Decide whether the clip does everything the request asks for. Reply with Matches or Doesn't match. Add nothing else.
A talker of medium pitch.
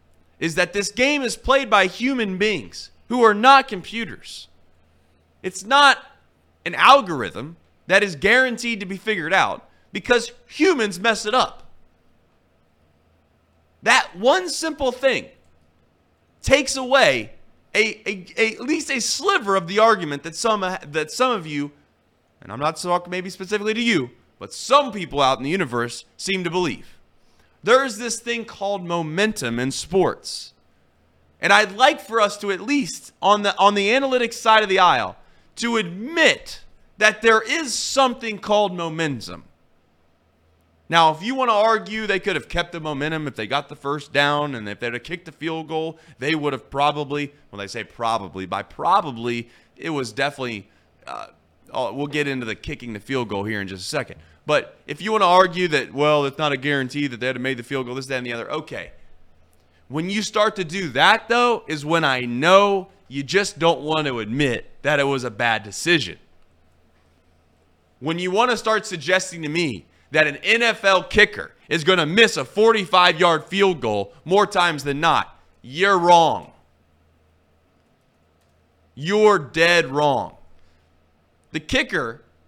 Matches